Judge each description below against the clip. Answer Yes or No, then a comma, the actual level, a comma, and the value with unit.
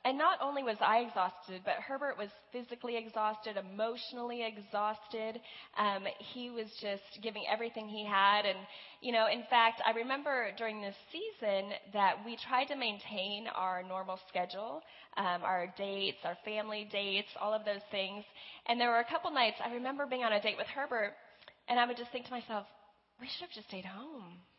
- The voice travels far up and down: No, average, 3.1 semitones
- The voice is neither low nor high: No, high, 215 Hz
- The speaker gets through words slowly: No, average, 185 wpm